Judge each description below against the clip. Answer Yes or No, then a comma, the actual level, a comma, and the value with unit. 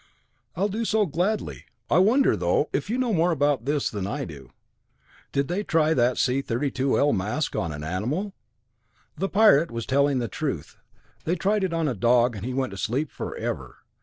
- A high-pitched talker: No, medium, 140 Hz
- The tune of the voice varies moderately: No, wide, 7.4 semitones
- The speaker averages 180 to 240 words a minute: Yes, average, 190 wpm